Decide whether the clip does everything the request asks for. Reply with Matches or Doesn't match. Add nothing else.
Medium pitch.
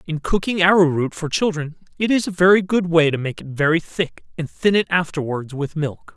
Matches